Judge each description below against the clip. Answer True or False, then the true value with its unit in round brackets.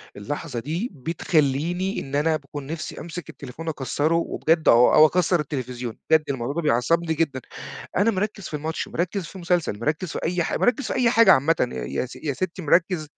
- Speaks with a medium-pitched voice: True (160 Hz)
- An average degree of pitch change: True (4.0 semitones)